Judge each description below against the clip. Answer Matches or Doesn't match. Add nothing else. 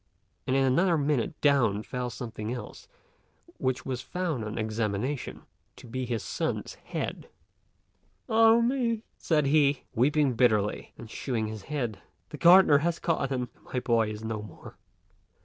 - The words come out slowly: Doesn't match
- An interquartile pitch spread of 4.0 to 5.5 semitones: Matches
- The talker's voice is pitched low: Matches